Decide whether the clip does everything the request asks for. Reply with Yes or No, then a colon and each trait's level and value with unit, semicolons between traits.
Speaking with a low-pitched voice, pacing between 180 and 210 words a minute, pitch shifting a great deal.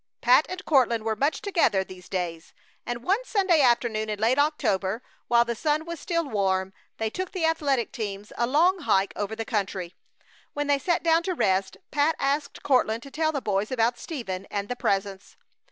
No: high, 240 Hz; average, 190 wpm; wide, 7.1 semitones